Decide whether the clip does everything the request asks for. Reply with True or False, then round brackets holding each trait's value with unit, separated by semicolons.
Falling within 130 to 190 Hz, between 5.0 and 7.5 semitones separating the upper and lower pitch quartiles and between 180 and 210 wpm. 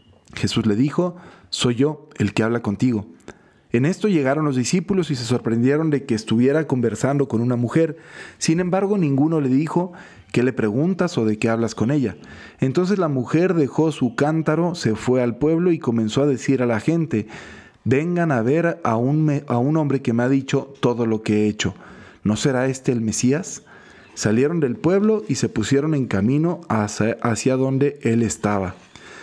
True (135 Hz; 5.3 semitones; 185 wpm)